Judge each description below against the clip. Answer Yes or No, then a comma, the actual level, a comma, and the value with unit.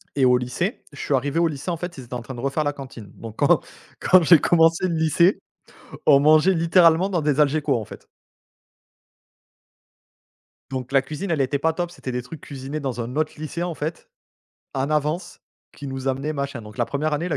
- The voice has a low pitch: No, medium, 150 Hz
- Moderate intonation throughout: Yes, average, 3.6 semitones